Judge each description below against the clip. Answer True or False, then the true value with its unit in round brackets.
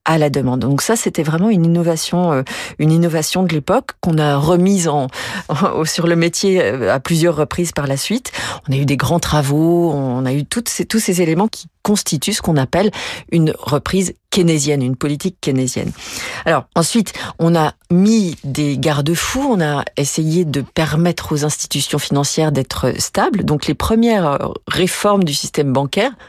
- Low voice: False (165 Hz)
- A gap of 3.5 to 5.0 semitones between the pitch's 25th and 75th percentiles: True (3.9 semitones)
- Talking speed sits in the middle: True (175 wpm)